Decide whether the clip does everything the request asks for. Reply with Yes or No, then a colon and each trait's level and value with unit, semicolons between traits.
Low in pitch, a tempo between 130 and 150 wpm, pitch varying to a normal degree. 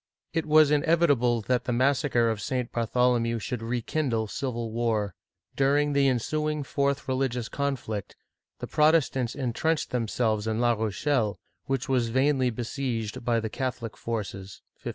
Yes: low, 125 Hz; average, 145 wpm; average, 3.5 semitones